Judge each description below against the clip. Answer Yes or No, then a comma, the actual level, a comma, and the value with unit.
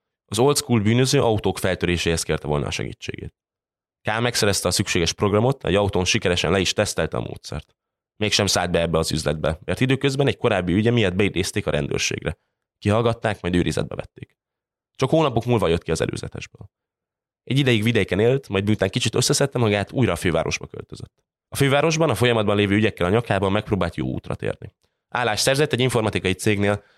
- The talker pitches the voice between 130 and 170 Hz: No, low, 105 Hz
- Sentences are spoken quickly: Yes, fast, 175 wpm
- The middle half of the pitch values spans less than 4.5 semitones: No, average, 4.9 semitones